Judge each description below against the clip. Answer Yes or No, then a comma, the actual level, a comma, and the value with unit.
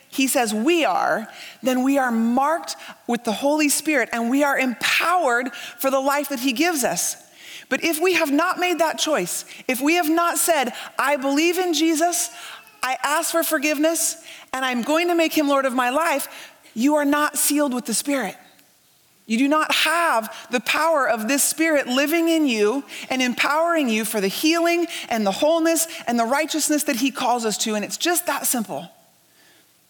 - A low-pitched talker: No, very high, 290 Hz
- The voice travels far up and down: No, average, 4.5 semitones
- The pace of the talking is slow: No, average, 190 wpm